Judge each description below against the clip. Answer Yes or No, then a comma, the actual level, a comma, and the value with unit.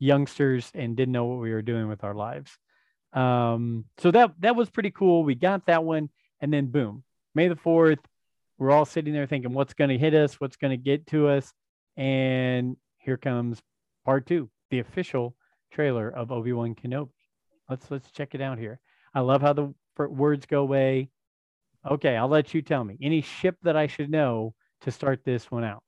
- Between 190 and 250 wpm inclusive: Yes, average, 200 wpm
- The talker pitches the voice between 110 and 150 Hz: Yes, low, 135 Hz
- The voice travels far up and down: No, average, 3.4 semitones